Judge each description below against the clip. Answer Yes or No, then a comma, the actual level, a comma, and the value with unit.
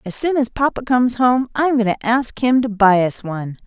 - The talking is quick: Yes, fast, 260 wpm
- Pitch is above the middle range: Yes, high, 235 Hz